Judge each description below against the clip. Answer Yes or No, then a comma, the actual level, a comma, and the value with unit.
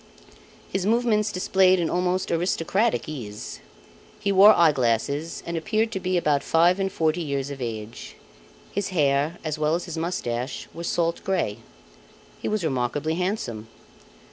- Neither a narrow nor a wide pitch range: Yes, average, 5.0 semitones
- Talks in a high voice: No, medium, 170 Hz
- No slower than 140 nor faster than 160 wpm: Yes, average, 150 wpm